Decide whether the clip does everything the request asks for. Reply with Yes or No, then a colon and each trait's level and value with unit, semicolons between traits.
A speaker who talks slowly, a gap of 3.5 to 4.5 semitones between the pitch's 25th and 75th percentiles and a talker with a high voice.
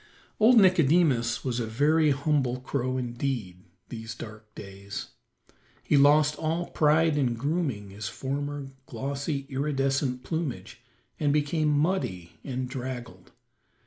No: slow, 115 wpm; average, 3.8 semitones; medium, 140 Hz